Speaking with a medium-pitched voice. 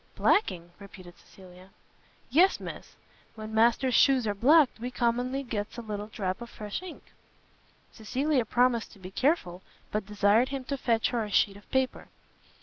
No: high, 230 Hz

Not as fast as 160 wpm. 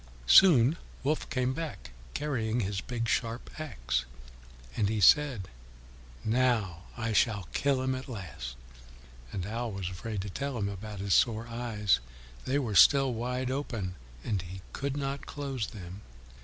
Yes: average, 150 wpm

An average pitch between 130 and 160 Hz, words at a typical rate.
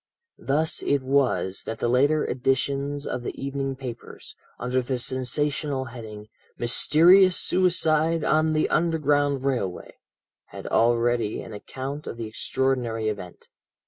No: low, 135 Hz; slow, 125 wpm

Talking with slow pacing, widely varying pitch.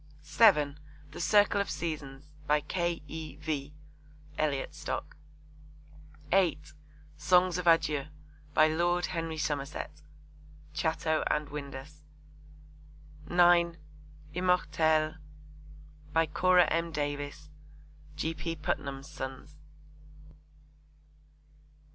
No: slow, 85 wpm; narrow, 2.5 semitones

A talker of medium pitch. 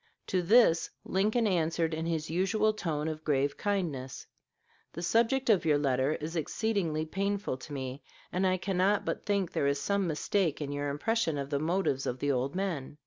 Yes: medium, 165 Hz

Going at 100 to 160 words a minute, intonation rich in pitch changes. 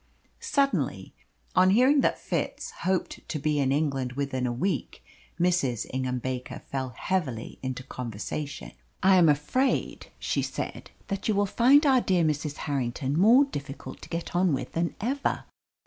Yes: average, 155 wpm; wide, 6.9 semitones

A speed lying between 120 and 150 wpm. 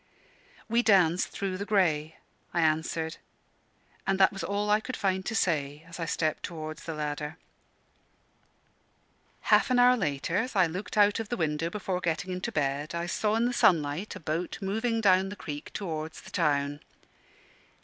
No: average, 170 wpm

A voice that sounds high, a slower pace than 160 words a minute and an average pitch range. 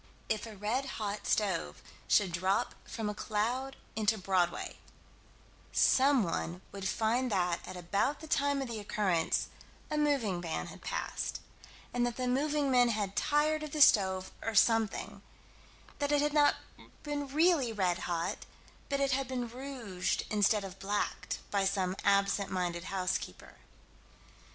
No: high, 220 Hz; average, 145 wpm; wide, 5.9 semitones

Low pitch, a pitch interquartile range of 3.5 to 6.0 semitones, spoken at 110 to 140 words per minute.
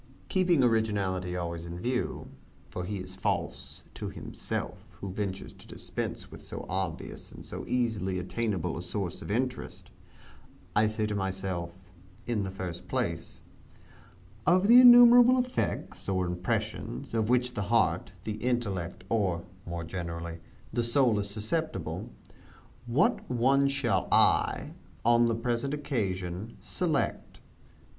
Yes: low, 105 Hz; average, 5.2 semitones; slow, 135 wpm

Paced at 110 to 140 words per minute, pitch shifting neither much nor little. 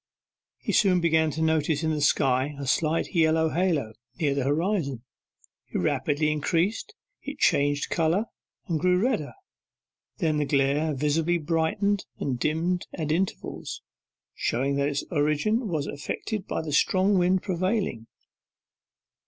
Yes: slow, 135 wpm; average, 3.8 semitones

